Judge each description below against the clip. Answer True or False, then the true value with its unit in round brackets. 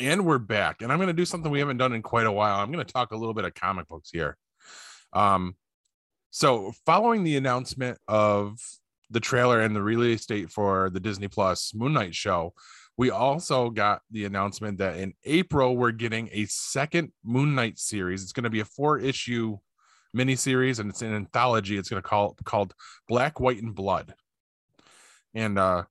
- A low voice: True (115 Hz)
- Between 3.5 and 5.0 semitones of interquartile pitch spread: True (3.9 semitones)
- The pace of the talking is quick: False (195 wpm)